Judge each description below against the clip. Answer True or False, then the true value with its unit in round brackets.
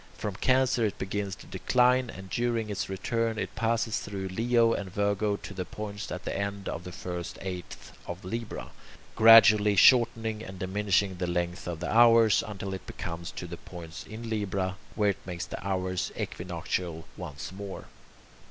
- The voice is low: True (100 Hz)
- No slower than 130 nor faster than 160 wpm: False (170 wpm)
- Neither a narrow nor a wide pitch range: True (3.4 semitones)